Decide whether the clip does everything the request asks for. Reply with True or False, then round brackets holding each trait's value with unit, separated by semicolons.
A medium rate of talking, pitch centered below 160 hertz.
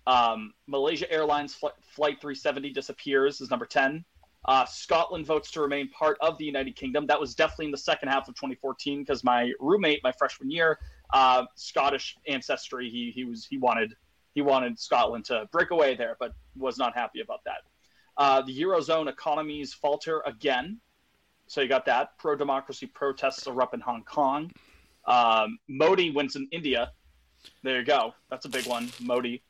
True (175 wpm; 140 Hz)